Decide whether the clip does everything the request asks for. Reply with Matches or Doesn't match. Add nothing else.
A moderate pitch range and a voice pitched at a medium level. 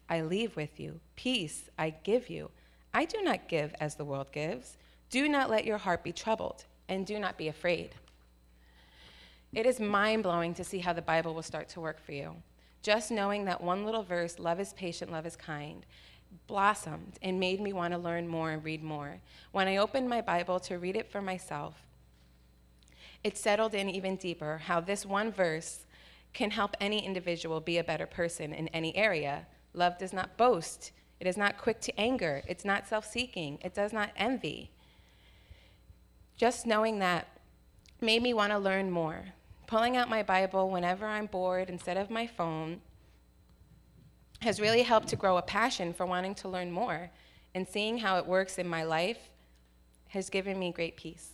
Matches